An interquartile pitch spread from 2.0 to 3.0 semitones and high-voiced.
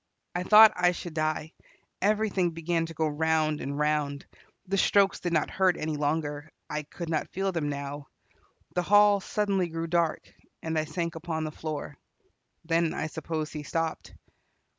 No: narrow, 2.6 semitones; medium, 160 Hz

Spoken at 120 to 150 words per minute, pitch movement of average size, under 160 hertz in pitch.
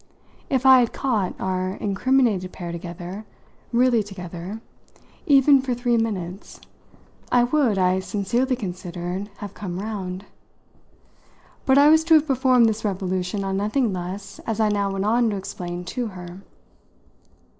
No: average, 145 wpm; average, 4.9 semitones; high, 205 Hz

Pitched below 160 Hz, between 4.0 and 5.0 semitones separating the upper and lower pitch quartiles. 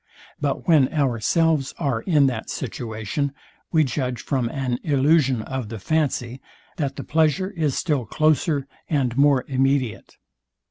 No: low, 135 Hz; average, 3.4 semitones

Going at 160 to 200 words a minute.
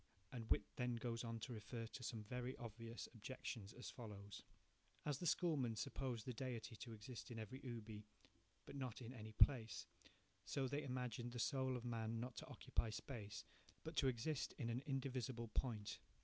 Yes: average, 180 wpm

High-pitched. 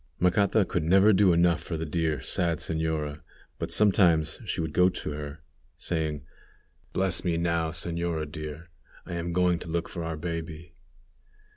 No: very low, 85 Hz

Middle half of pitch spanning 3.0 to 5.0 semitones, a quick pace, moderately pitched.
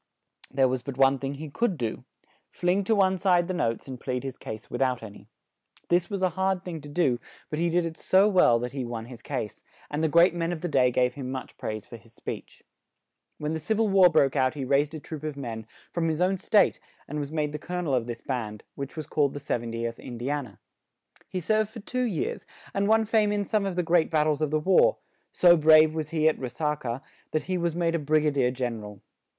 No: wide, 5.5 semitones; fast, 255 wpm; medium, 150 Hz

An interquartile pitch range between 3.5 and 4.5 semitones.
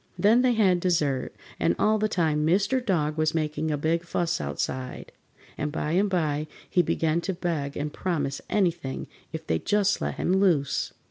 Yes: average, 4.1 semitones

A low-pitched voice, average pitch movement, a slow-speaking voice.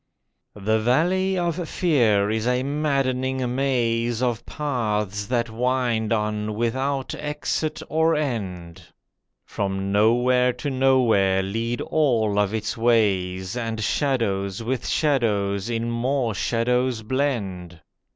Yes: low, 115 Hz; average, 3.9 semitones; slow, 110 wpm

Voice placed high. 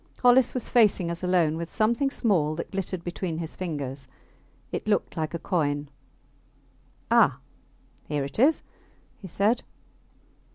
No: medium, 175 Hz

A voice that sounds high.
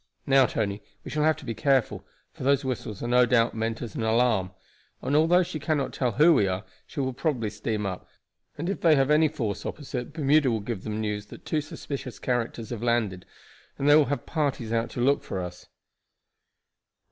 No: low, 125 Hz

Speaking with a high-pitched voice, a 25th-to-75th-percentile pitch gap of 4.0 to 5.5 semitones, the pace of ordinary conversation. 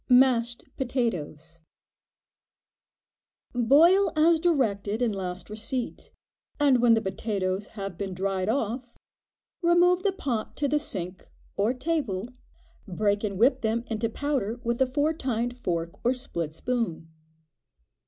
No: high, 235 Hz; average, 5.2 semitones; slow, 130 wpm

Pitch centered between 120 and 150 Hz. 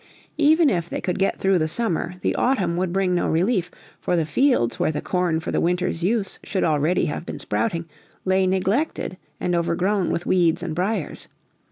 No: medium, 180 Hz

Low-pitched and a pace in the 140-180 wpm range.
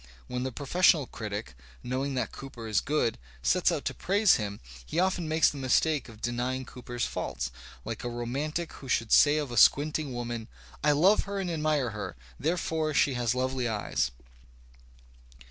Yes: low, 130 Hz; average, 170 wpm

